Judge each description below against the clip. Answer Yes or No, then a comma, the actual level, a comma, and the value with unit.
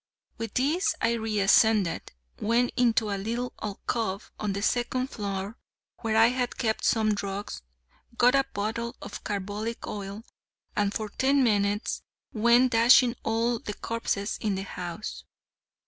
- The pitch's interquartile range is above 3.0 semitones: No, average, 2.7 semitones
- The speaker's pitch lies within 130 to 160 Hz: No, high, 220 Hz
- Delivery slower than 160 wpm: Yes, average, 145 wpm